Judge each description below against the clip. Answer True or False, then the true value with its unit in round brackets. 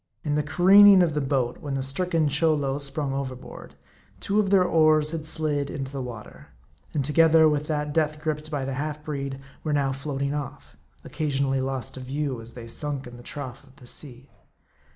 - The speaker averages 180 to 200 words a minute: True (195 wpm)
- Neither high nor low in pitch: True (145 Hz)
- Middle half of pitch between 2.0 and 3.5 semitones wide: True (2.4 semitones)